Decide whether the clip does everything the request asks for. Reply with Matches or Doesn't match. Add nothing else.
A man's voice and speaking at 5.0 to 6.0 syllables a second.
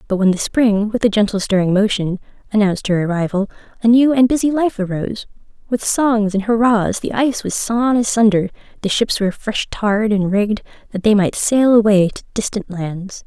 Doesn't match